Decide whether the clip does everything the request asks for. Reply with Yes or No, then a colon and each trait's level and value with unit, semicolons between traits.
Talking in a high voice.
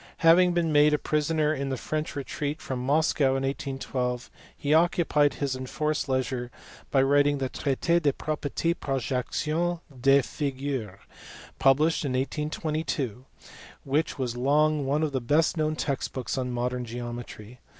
No: medium, 140 Hz